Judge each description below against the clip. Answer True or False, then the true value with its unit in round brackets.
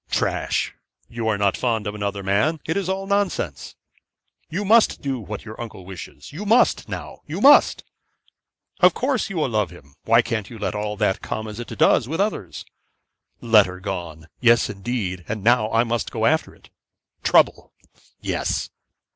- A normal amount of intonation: False (6.2 semitones)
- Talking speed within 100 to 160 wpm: False (170 wpm)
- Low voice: True (110 Hz)